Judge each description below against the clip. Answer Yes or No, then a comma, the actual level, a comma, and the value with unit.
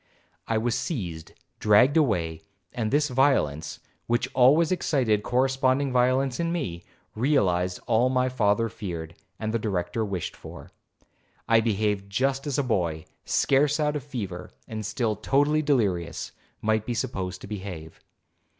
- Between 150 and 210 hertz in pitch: No, low, 115 Hz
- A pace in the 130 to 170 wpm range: Yes, average, 145 wpm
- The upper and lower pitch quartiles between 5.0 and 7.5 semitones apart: Yes, wide, 5.5 semitones